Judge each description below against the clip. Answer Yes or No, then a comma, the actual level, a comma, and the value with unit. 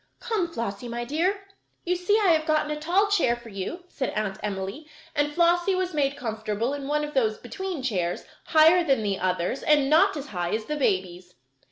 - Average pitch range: No, wide, 7.9 semitones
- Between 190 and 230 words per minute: Yes, average, 200 wpm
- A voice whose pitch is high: Yes, very high, 285 Hz